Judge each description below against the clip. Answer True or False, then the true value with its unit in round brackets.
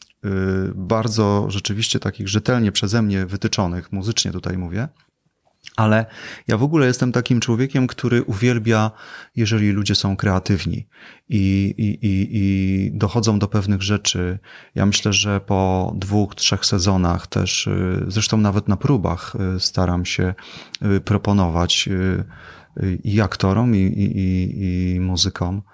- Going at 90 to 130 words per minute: True (120 wpm)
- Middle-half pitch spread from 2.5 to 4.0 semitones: True (2.8 semitones)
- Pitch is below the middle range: True (100 Hz)